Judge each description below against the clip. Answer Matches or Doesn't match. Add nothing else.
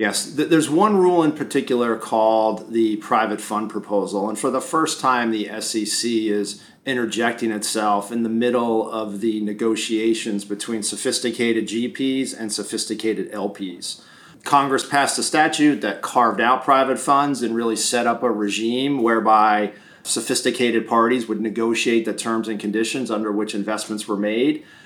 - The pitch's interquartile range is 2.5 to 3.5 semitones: Matches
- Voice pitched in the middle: Doesn't match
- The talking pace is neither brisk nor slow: Matches